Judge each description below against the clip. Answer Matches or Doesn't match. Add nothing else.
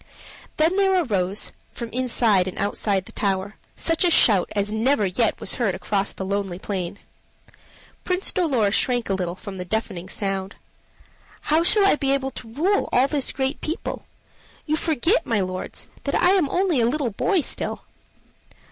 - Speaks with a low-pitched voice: Doesn't match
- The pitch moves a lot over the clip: Matches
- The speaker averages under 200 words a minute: Matches